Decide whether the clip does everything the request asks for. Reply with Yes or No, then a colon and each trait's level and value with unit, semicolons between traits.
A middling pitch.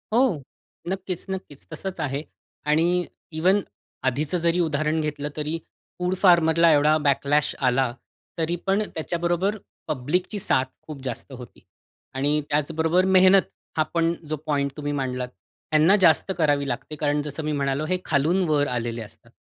Yes: medium, 155 Hz